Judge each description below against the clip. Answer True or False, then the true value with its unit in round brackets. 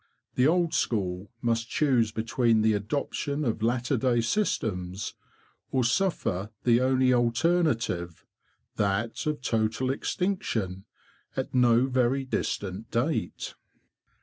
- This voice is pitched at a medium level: False (120 Hz)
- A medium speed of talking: False (105 wpm)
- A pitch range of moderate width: True (3.5 semitones)